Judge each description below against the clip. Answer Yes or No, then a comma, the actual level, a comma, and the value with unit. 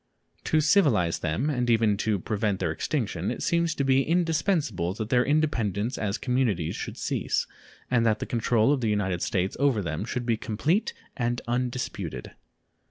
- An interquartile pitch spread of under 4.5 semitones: No, average, 4.8 semitones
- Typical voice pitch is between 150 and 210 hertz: No, low, 115 Hz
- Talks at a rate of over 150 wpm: Yes, average, 165 wpm